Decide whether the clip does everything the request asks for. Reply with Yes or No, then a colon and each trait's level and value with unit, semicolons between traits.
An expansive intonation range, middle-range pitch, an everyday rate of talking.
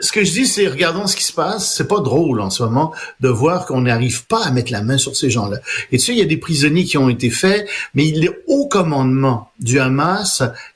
No: wide, 6.8 semitones; medium, 145 Hz; fast, 260 wpm